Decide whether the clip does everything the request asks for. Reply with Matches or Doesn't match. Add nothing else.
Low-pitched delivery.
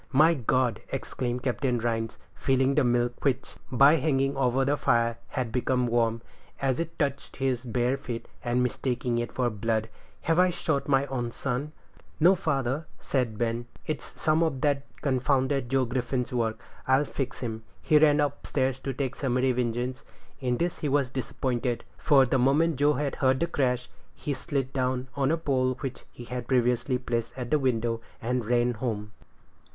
Matches